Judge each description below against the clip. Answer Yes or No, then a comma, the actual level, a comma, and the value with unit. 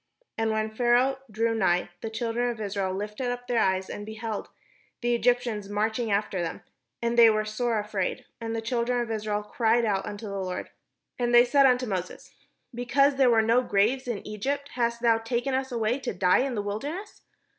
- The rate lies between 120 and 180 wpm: No, average, 195 wpm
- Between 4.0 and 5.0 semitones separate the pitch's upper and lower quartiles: No, average, 2.7 semitones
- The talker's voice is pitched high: Yes, high, 225 Hz